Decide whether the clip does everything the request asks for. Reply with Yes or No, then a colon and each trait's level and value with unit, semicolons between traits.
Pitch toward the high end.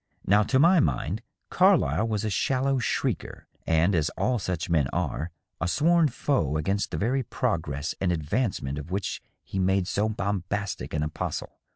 No: low, 100 Hz